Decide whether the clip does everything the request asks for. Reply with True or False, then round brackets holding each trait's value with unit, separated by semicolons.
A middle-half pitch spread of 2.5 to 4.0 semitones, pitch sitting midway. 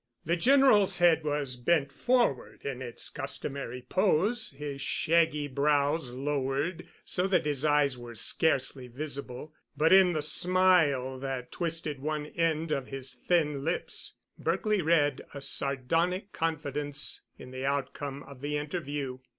True (3.4 semitones; 145 Hz)